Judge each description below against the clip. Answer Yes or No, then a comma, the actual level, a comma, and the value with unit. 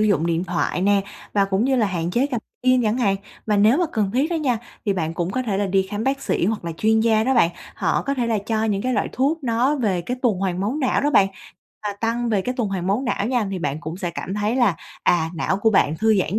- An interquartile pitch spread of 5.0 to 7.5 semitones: No, average, 4.3 semitones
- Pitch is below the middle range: No, high, 210 Hz